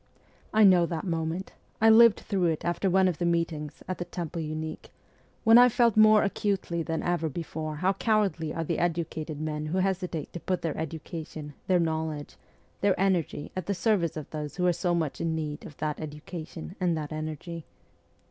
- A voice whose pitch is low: No, medium, 170 Hz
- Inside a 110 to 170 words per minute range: No, average, 190 wpm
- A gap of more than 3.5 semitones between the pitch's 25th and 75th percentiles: No, average, 3.1 semitones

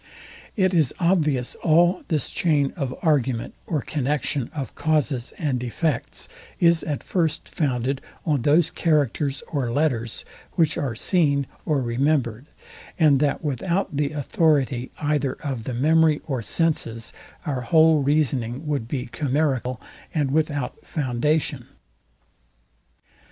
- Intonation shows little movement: No, average, 3.5 semitones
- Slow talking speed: Yes, slow, 125 wpm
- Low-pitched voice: No, medium, 145 Hz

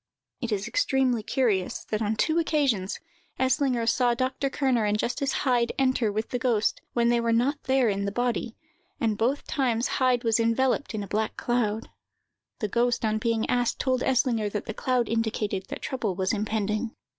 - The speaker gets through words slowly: No, average, 180 wpm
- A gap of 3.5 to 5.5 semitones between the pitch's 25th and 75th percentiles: No, average, 3.1 semitones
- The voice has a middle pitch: No, high, 235 Hz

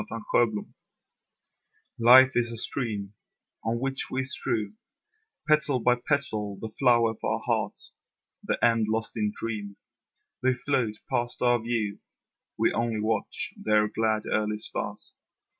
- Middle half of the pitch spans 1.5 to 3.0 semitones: Yes, narrow, 2.6 semitones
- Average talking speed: No, slow, 130 wpm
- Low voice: Yes, low, 115 Hz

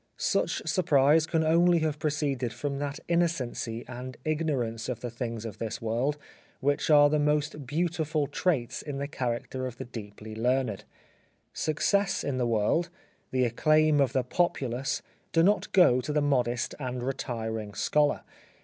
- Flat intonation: No, average, 4.2 semitones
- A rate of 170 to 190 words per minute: No, average, 160 wpm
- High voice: No, low, 135 Hz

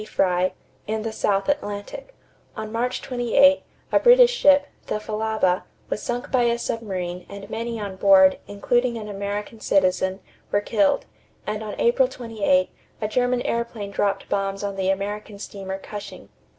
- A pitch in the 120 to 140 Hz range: No, high, 210 Hz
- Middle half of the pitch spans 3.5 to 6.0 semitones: No, average, 3.1 semitones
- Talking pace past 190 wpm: No, average, 150 wpm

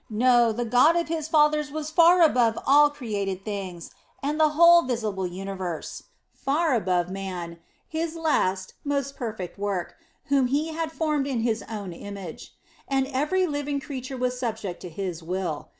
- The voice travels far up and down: Yes, wide, 7.4 semitones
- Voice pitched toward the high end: Yes, very high, 250 Hz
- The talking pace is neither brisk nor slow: Yes, average, 160 wpm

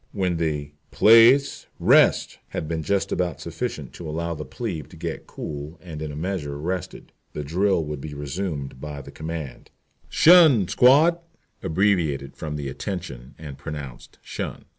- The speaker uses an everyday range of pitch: Yes, average, 4.5 semitones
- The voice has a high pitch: No, very low, 80 Hz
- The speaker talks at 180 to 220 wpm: No, average, 150 wpm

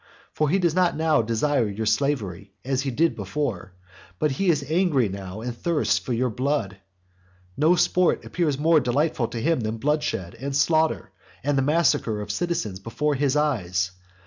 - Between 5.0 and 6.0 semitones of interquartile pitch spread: Yes, wide, 5.6 semitones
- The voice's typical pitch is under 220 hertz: Yes, medium, 140 Hz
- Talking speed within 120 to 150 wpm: No, average, 175 wpm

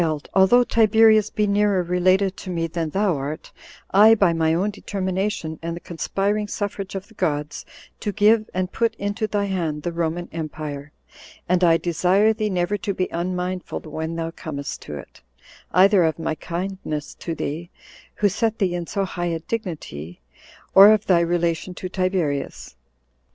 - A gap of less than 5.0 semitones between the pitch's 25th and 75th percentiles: Yes, average, 3.6 semitones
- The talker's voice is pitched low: No, medium, 180 Hz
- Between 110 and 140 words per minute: No, average, 165 wpm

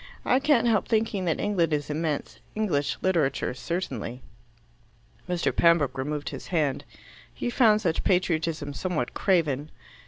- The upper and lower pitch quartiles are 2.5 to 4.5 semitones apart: No, average, 4.9 semitones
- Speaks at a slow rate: Yes, slow, 130 wpm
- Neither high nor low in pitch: Yes, medium, 165 Hz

